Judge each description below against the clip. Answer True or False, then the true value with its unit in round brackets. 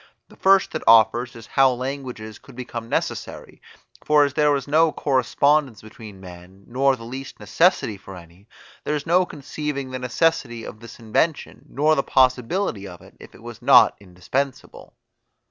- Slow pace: False (165 wpm)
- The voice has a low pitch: True (130 Hz)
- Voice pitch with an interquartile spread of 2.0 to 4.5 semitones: False (4.9 semitones)